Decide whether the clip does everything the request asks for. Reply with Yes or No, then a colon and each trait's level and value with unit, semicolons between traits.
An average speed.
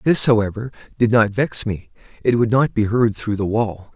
No: fast, 210 wpm